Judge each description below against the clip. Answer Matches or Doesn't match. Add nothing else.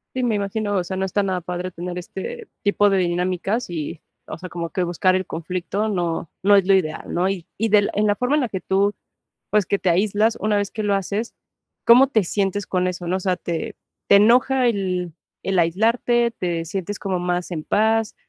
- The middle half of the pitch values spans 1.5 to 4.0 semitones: Matches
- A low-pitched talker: Doesn't match